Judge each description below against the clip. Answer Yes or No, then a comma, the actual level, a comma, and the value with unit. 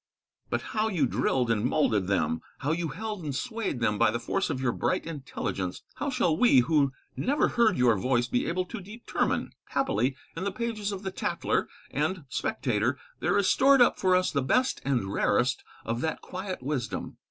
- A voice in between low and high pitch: Yes, medium, 150 Hz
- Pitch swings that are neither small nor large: No, wide, 8.5 semitones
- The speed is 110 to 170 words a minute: No, average, 190 wpm